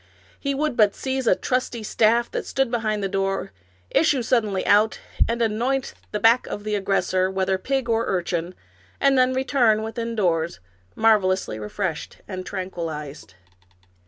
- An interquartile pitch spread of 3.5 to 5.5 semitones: Yes, average, 4.2 semitones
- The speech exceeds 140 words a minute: Yes, average, 150 wpm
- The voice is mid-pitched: No, high, 215 Hz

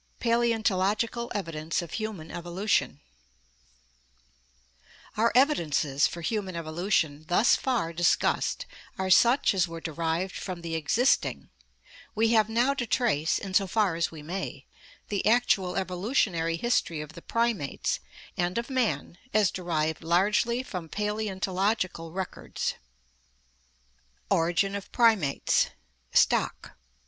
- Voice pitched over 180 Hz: Yes, high, 190 Hz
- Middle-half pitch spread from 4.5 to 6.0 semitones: Yes, average, 4.9 semitones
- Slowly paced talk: Yes, slow, 115 wpm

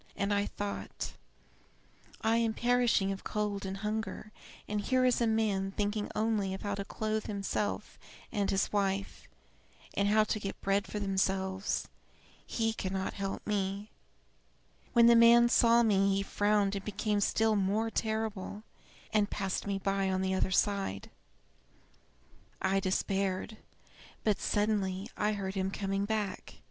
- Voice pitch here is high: Yes, high, 205 Hz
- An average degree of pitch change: No, narrow, 1.9 semitones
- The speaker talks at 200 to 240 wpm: No, average, 145 wpm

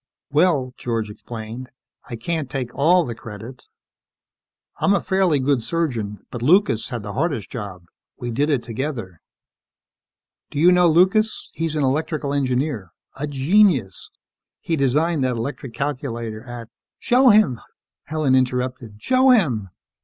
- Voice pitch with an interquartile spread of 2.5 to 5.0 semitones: No, wide, 5.5 semitones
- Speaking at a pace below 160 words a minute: Yes, average, 140 wpm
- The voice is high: No, low, 135 Hz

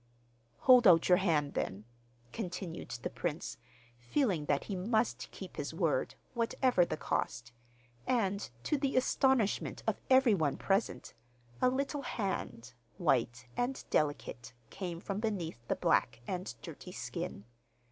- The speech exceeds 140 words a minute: No, slow, 135 wpm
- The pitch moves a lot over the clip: Yes, wide, 7.7 semitones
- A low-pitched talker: No, high, 190 Hz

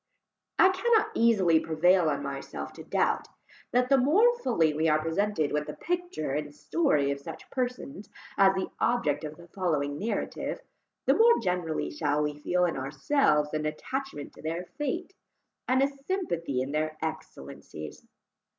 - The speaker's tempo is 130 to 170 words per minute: Yes, average, 160 wpm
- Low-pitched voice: No, medium, 170 Hz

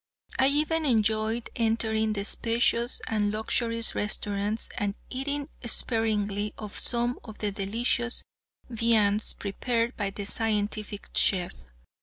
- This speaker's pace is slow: Yes, slow, 115 wpm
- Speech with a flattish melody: Yes, narrow, 2.3 semitones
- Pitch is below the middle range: No, high, 220 Hz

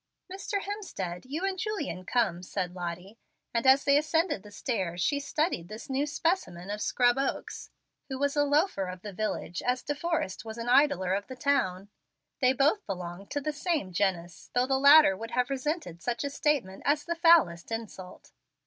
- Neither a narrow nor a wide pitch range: No, wide, 7.7 semitones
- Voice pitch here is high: Yes, very high, 250 Hz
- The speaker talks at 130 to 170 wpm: No, average, 185 wpm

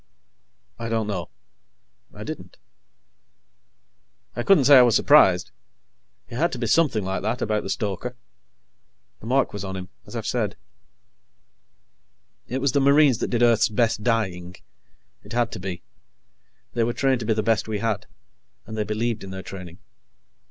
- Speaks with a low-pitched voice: Yes, low, 115 Hz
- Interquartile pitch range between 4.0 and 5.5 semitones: No, average, 3.2 semitones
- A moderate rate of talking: Yes, average, 165 wpm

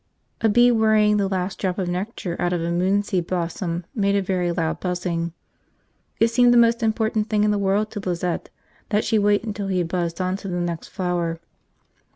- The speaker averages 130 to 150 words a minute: No, average, 200 wpm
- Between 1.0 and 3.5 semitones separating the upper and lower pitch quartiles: Yes, average, 3.1 semitones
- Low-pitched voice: No, high, 190 Hz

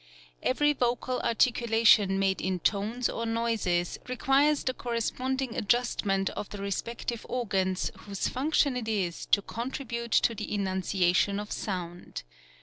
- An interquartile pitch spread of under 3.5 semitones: No, average, 4.1 semitones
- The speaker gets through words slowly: Yes, slow, 130 wpm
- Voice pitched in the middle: No, high, 225 Hz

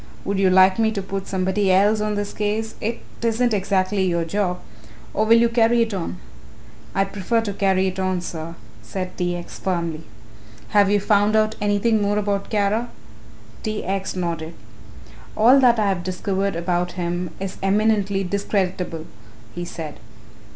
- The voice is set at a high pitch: Yes, high, 195 Hz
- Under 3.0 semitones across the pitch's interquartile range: Yes, narrow, 2.5 semitones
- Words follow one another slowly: No, average, 165 wpm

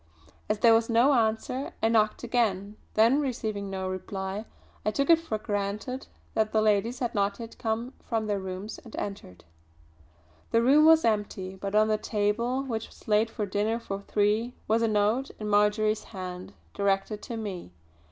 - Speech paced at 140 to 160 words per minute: No, average, 175 wpm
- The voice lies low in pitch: No, high, 215 Hz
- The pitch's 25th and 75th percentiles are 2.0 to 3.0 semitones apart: Yes, narrow, 2.4 semitones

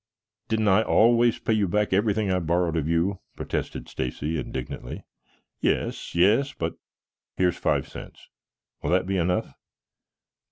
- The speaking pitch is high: No, very low, 95 Hz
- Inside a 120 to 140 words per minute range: Yes, slow, 135 wpm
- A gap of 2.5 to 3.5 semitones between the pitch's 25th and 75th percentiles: No, average, 4.2 semitones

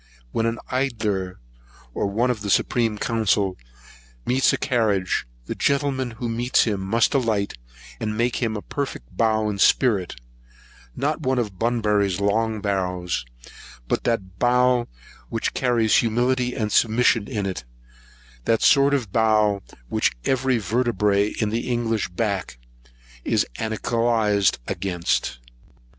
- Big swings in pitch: No, average, 3.2 semitones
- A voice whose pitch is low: Yes, low, 110 Hz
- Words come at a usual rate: No, slow, 130 wpm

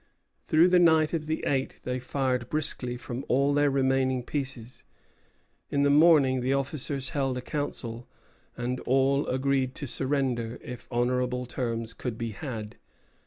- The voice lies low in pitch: Yes, low, 130 Hz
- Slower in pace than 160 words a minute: Yes, average, 150 wpm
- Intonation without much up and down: Yes, narrow, 2.3 semitones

